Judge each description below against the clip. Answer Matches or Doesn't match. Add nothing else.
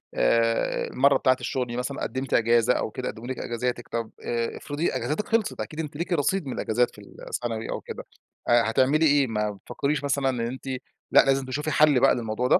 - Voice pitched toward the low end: Matches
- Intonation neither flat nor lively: Matches